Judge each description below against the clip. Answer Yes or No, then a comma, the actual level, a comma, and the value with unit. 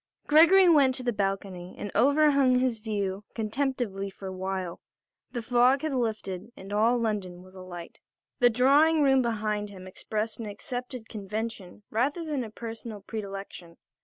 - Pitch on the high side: Yes, high, 220 Hz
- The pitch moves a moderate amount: Yes, average, 4.6 semitones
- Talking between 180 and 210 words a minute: No, average, 155 wpm